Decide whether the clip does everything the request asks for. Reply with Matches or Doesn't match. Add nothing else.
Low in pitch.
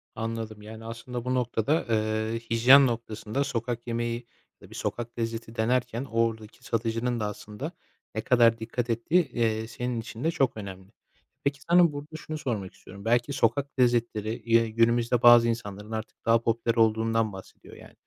Matches